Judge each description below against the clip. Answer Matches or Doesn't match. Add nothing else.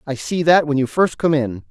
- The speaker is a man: Matches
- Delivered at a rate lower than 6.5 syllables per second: Matches